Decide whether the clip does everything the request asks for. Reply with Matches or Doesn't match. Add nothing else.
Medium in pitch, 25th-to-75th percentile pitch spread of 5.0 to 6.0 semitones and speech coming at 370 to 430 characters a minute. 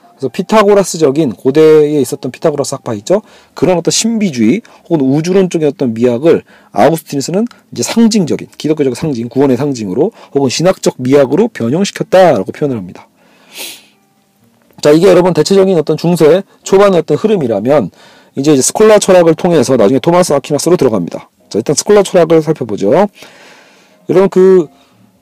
Matches